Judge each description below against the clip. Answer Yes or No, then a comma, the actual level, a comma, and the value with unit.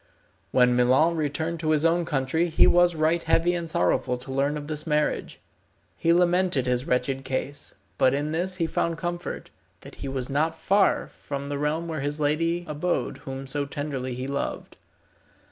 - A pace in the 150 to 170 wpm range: No, average, 180 wpm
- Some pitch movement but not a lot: Yes, average, 3.6 semitones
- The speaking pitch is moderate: Yes, medium, 150 Hz